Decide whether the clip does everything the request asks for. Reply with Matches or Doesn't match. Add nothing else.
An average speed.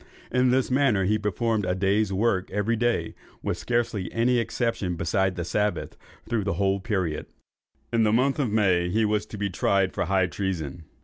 Matches